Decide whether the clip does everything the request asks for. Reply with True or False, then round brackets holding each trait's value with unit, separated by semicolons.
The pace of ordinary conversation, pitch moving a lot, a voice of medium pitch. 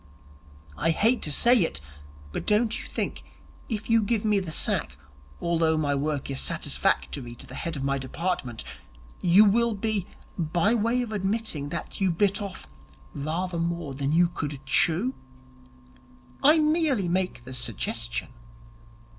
True (155 wpm; 6.9 semitones; 175 Hz)